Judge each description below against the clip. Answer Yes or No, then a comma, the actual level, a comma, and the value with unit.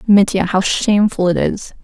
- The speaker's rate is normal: Yes, average, 165 wpm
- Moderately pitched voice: No, high, 195 Hz